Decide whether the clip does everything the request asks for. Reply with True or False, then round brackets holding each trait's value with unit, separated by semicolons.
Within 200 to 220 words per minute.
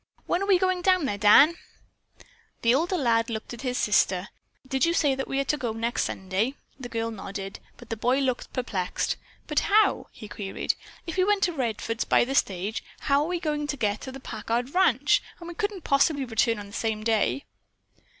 True (205 wpm)